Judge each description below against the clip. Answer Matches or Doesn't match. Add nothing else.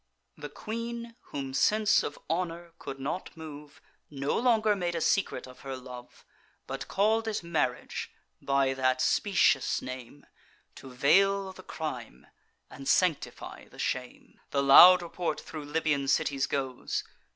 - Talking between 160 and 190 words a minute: Doesn't match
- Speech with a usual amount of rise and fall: Doesn't match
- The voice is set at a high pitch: Doesn't match